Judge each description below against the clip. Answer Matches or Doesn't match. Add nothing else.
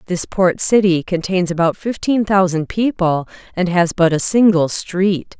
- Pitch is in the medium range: Matches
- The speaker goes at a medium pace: Matches